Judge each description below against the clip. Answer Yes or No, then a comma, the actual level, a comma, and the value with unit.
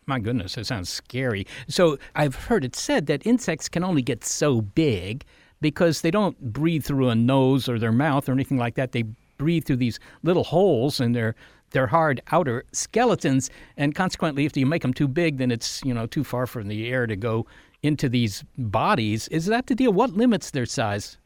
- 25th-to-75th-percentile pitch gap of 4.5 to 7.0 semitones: Yes, average, 4.9 semitones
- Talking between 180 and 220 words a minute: Yes, fast, 205 wpm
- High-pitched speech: No, low, 135 Hz